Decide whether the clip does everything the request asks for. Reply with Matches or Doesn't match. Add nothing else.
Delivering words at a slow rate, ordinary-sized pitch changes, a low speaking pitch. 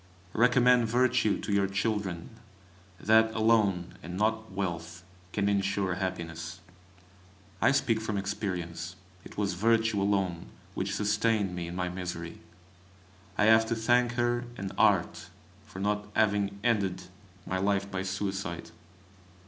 Matches